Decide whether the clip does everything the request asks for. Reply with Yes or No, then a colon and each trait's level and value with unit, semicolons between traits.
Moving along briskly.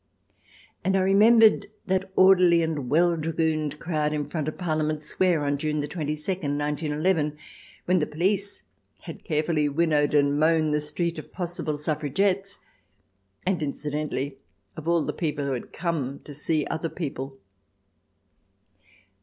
No: average, 145 wpm